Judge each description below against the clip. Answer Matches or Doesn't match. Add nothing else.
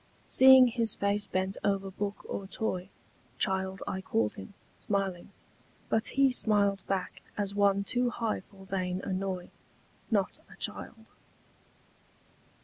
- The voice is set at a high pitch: Matches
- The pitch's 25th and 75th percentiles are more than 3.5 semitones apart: Doesn't match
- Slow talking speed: Matches